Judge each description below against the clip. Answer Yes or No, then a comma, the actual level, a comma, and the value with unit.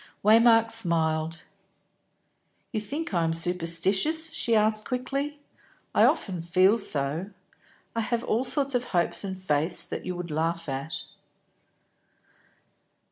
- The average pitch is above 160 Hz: Yes, high, 190 Hz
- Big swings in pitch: Yes, wide, 5.8 semitones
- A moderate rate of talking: No, slow, 125 wpm